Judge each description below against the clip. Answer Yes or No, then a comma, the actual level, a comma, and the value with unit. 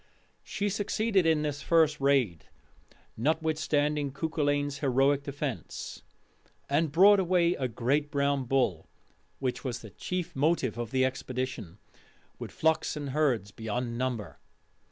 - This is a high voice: No, medium, 140 Hz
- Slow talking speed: Yes, slow, 125 wpm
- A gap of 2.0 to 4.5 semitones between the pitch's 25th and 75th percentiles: Yes, average, 3.7 semitones